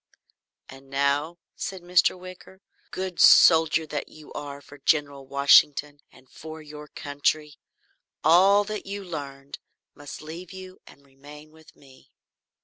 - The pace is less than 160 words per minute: Yes, slow, 135 wpm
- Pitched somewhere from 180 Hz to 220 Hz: No, medium, 150 Hz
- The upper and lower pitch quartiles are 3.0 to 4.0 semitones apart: Yes, average, 3.7 semitones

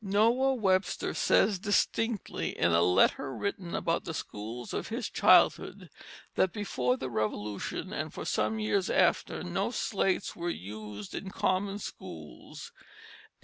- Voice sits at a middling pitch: Yes, medium, 170 Hz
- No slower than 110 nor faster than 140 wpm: Yes, slow, 135 wpm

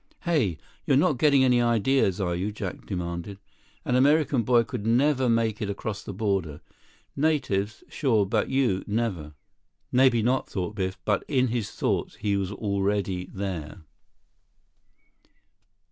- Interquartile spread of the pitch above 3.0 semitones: Yes, average, 4.8 semitones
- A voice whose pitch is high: No, low, 105 Hz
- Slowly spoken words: Yes, slow, 130 wpm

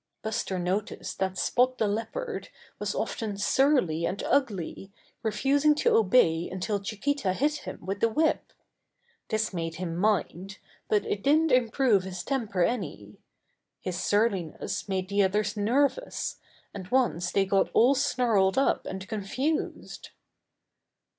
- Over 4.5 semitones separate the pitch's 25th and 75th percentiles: Yes, average, 5.1 semitones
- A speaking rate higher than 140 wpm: No, slow, 135 wpm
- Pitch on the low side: No, high, 210 Hz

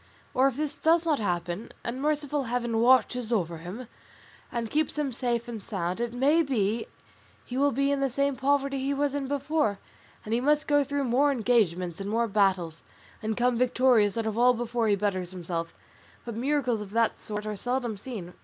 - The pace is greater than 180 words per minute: Yes, average, 195 wpm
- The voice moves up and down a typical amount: Yes, average, 4.7 semitones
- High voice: Yes, high, 240 Hz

